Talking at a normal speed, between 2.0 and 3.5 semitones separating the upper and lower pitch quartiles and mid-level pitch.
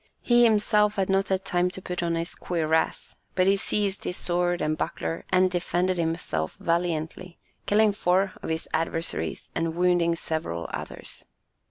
Yes: average, 160 wpm; narrow, 2.6 semitones; medium, 180 Hz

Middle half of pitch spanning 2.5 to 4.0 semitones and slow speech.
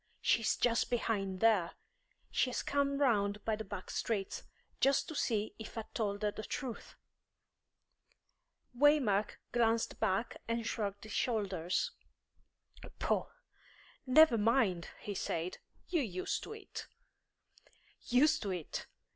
Yes: average, 3.6 semitones; slow, 130 wpm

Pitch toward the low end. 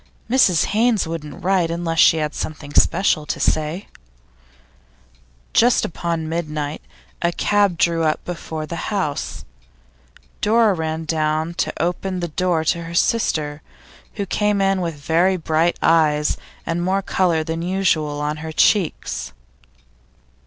No: medium, 165 Hz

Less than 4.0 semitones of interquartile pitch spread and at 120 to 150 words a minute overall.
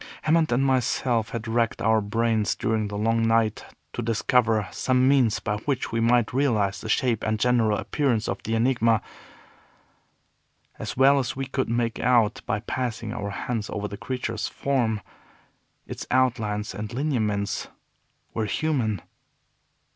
Yes: average, 2.8 semitones; average, 145 wpm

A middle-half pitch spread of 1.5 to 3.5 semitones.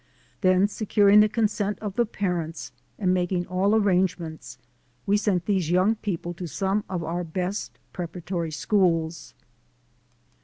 Yes: average, 2.8 semitones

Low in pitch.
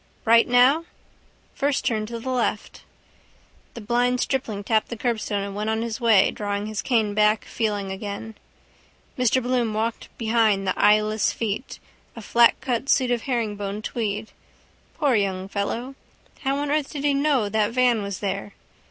No: high, 225 Hz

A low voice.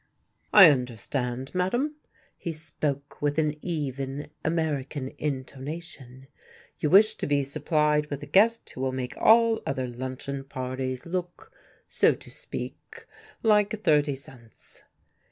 No: medium, 145 Hz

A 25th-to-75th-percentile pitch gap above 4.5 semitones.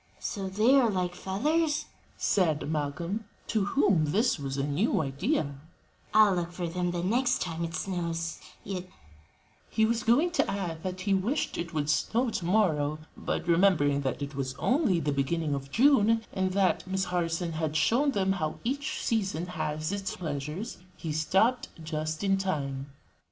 Yes: average, 5.3 semitones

